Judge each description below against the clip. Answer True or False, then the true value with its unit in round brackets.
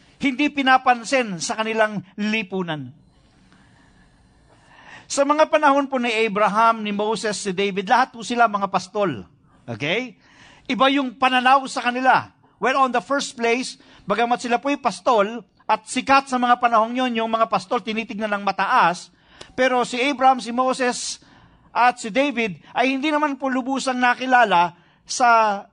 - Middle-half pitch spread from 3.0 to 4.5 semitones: True (3.4 semitones)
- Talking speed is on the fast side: False (145 wpm)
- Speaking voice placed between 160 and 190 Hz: False (240 Hz)